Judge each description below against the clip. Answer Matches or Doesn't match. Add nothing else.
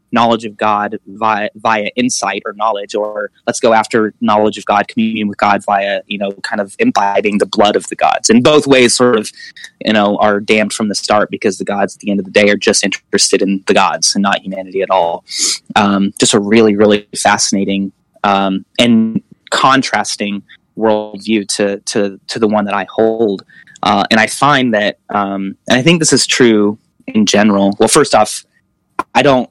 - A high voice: Doesn't match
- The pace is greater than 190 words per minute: Matches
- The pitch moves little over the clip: Matches